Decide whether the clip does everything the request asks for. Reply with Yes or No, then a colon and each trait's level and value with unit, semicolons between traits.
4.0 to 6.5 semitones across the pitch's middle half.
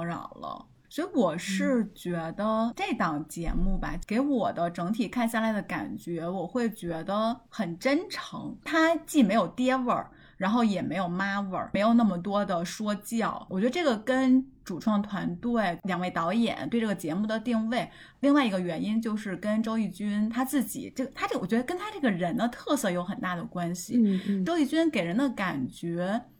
Yes: wide, 5.4 semitones